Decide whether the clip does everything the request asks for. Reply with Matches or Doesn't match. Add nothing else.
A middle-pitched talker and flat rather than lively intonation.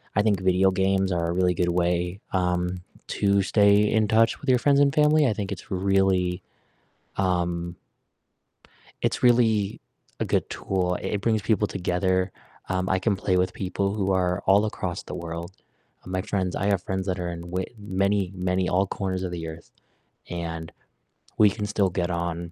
Doesn't match